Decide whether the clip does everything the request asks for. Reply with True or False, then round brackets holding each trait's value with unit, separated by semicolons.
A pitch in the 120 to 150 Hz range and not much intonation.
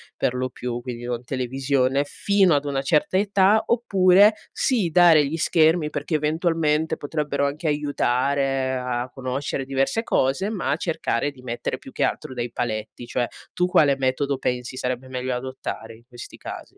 False (140 Hz; 4.0 semitones)